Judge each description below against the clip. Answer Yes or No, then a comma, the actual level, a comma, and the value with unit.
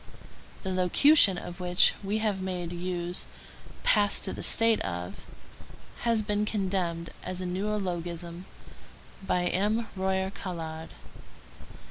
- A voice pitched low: No, medium, 185 Hz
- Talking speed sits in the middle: No, slow, 105 wpm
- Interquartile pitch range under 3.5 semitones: Yes, average, 2.7 semitones